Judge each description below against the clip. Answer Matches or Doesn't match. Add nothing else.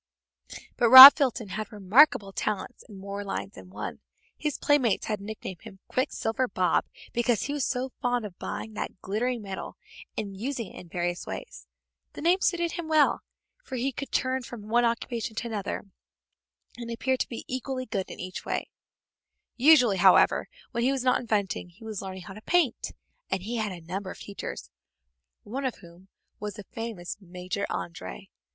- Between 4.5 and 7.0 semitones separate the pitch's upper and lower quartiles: Matches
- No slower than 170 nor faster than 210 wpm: Matches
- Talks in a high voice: Matches